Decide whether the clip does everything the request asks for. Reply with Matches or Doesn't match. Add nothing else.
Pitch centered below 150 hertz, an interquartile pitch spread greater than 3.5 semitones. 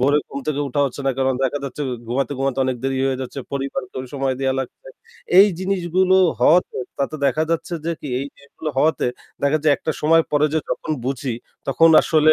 Doesn't match